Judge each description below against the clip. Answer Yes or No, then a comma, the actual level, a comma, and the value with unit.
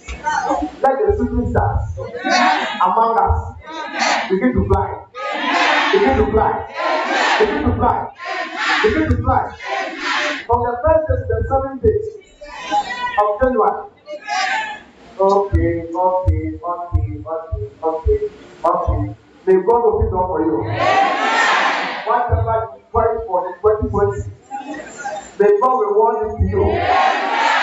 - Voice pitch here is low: No, high, 235 Hz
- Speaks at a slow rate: Yes, slow, 130 wpm